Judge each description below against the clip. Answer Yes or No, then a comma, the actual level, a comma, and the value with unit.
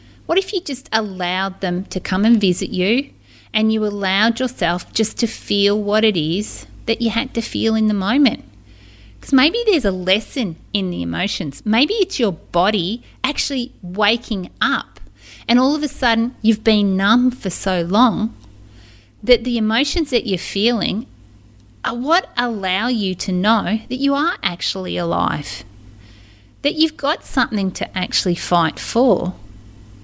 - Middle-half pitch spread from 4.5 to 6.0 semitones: Yes, average, 5.2 semitones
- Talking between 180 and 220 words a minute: No, average, 160 wpm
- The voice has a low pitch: No, high, 215 Hz